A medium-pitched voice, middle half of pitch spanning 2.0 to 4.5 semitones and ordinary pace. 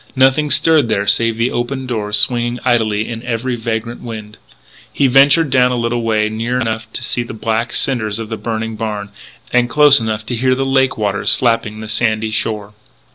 No: low, 115 Hz; narrow, 2.4 semitones; average, 190 wpm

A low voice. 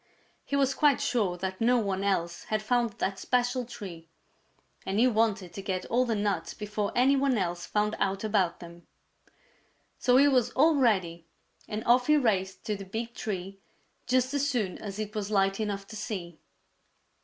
No: high, 210 Hz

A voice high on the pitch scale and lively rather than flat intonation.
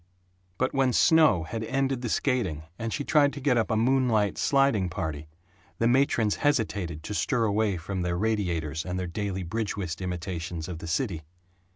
No: low, 105 Hz; wide, 6.3 semitones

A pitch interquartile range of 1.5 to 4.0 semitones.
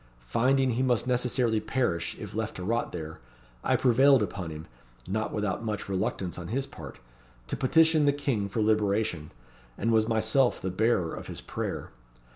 No: average, 4.8 semitones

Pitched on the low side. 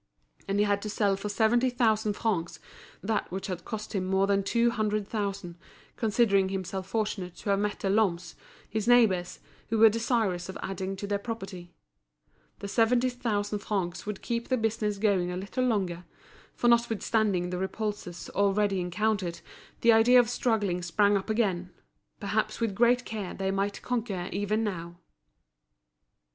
No: high, 205 Hz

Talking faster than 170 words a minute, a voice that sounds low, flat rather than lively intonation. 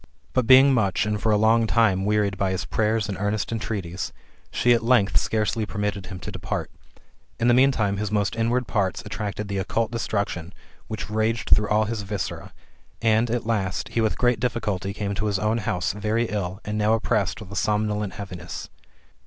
Yes: average, 190 wpm; low, 105 Hz; narrow, 2.2 semitones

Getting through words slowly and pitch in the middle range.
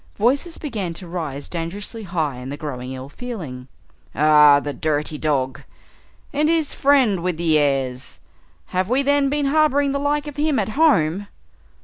No: average, 165 wpm; medium, 180 Hz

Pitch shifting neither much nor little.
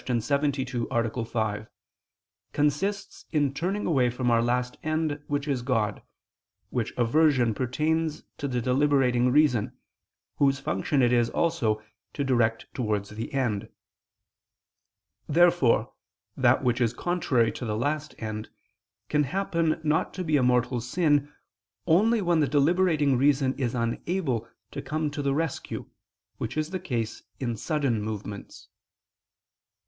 Yes: average, 4.5 semitones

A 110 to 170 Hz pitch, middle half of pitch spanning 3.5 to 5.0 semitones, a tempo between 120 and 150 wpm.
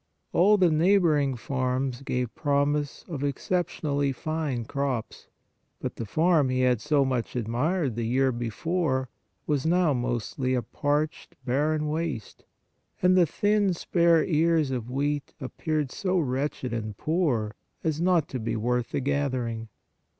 Yes: medium, 140 Hz; average, 4.2 semitones; average, 145 wpm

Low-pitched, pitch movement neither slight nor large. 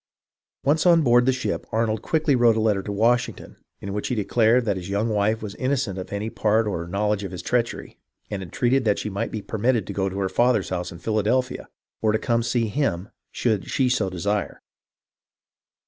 Yes: low, 110 Hz; average, 3.4 semitones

